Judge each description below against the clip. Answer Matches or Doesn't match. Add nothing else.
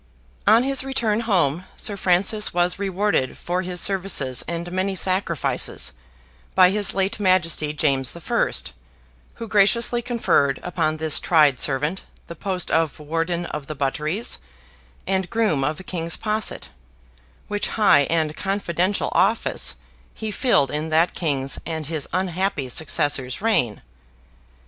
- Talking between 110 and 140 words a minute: Matches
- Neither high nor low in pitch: Matches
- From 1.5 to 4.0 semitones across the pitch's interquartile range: Doesn't match